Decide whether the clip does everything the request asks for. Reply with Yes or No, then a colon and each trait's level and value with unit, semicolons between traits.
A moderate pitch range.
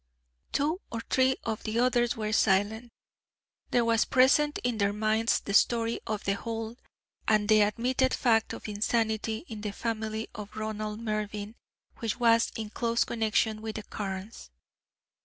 No: narrow, 1.6 semitones